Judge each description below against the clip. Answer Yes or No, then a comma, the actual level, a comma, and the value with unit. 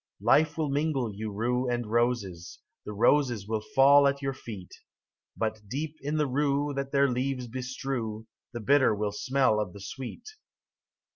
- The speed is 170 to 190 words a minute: No, average, 160 wpm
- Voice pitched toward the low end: Yes, low, 125 Hz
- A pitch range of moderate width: Yes, average, 4.2 semitones